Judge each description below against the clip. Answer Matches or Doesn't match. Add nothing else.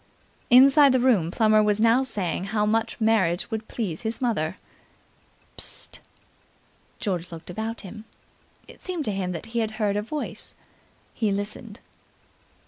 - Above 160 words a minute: Doesn't match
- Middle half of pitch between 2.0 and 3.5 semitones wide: Matches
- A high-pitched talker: Matches